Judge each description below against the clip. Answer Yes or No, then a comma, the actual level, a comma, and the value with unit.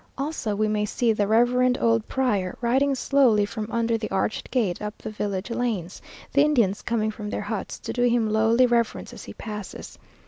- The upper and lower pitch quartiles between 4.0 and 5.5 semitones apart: No, average, 2.7 semitones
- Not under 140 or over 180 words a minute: No, average, 195 wpm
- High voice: Yes, high, 225 Hz